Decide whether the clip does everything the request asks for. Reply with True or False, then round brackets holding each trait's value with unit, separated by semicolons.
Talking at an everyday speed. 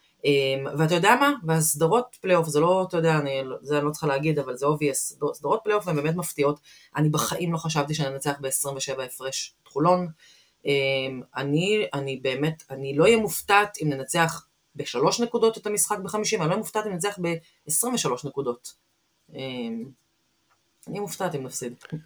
False (170 wpm)